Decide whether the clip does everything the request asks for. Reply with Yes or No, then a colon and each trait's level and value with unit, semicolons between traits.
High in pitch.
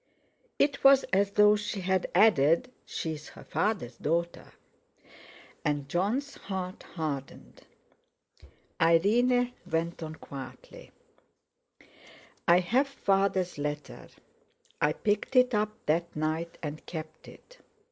No: medium, 180 Hz